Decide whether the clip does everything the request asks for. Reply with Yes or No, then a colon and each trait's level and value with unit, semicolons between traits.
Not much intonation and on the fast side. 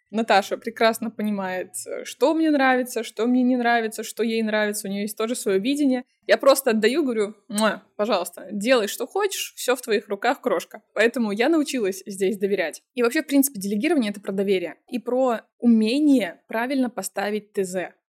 No: average, 3.7 semitones; fast, 170 wpm